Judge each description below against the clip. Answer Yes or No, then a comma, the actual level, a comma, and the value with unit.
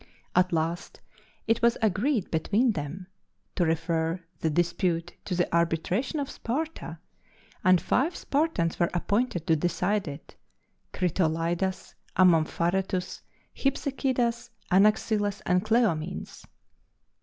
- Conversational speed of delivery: No, slow, 105 wpm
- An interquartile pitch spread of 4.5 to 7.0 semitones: Yes, average, 5.2 semitones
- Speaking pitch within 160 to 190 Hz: Yes, medium, 185 Hz